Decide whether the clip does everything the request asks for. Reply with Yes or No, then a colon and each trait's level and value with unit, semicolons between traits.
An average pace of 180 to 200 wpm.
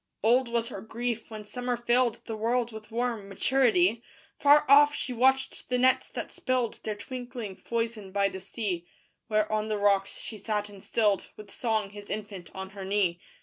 Yes: average, 185 wpm